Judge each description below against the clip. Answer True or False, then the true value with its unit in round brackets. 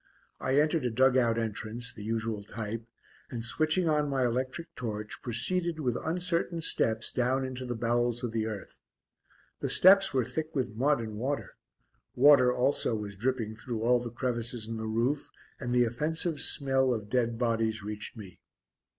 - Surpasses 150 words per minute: True (170 wpm)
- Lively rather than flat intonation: False (3.5 semitones)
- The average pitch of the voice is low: True (120 Hz)